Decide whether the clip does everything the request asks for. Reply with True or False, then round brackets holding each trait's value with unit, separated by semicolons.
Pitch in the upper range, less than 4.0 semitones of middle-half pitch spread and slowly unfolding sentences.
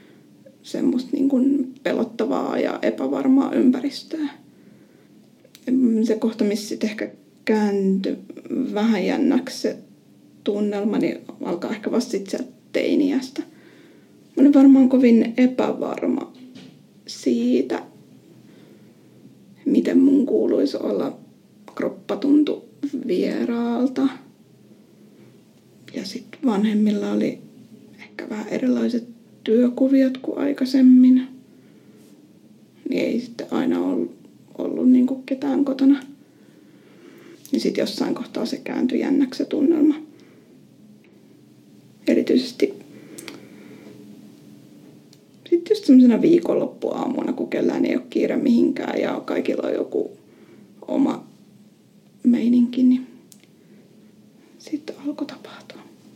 True (260 Hz; 3.4 semitones; 90 wpm)